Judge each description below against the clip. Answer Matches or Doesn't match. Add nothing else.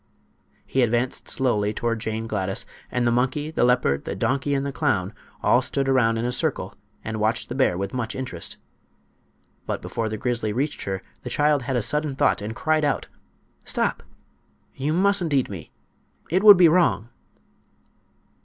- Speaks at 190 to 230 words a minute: Doesn't match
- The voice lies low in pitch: Matches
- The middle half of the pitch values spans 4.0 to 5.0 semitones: Matches